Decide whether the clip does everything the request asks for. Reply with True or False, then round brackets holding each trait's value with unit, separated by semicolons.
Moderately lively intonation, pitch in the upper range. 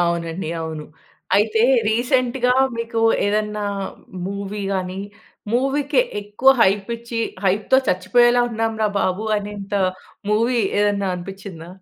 True (3.4 semitones; 210 Hz)